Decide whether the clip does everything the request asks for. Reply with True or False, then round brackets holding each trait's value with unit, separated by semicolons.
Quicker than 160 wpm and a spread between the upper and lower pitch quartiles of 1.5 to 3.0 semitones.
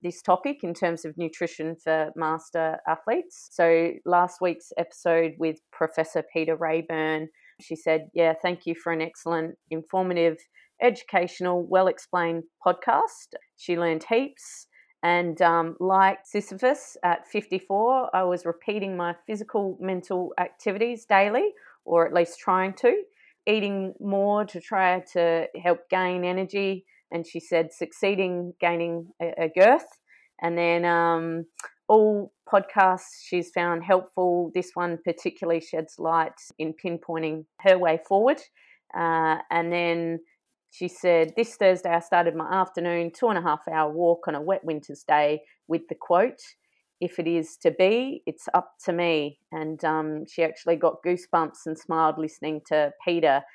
False (145 wpm; 2.5 semitones)